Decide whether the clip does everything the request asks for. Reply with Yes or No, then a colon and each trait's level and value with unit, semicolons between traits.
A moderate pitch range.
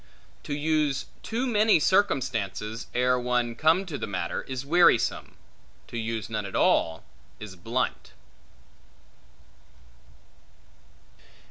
No: wide, 6.0 semitones